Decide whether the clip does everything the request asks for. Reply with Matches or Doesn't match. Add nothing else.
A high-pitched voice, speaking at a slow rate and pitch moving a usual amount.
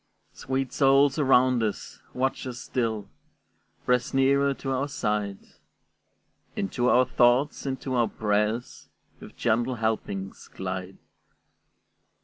Doesn't match